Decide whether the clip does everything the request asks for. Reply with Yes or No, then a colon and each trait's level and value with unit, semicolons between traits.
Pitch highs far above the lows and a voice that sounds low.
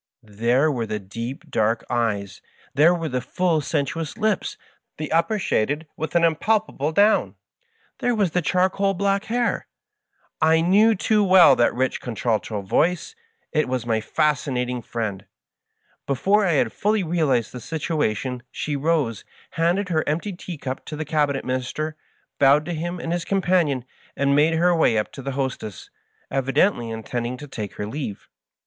No: wide, 5.9 semitones; medium, 150 Hz